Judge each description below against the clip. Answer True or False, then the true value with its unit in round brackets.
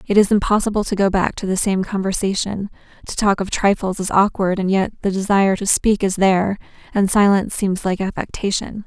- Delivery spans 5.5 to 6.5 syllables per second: True (5.7 syllables/s)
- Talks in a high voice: True (195 Hz)